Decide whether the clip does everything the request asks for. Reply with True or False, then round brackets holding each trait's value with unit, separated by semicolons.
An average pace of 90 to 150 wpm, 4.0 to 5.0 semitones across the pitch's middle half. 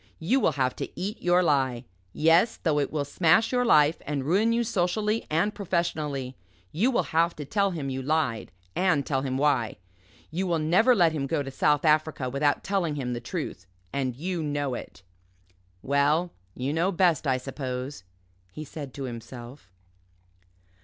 False (175 wpm; 4.6 semitones)